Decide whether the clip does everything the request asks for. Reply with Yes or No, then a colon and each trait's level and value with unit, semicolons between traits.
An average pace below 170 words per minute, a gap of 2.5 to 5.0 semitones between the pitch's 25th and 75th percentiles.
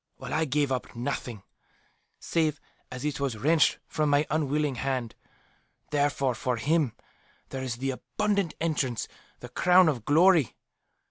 Yes: average, 140 wpm; average, 3.5 semitones